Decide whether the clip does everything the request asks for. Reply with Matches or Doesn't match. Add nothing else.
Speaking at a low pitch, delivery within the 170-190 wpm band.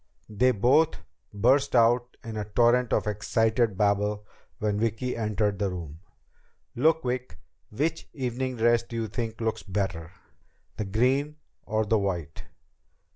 Doesn't match